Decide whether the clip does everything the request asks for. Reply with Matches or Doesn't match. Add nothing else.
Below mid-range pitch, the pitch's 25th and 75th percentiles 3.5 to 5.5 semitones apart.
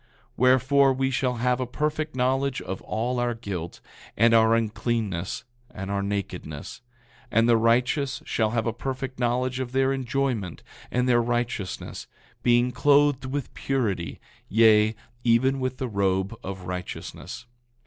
Doesn't match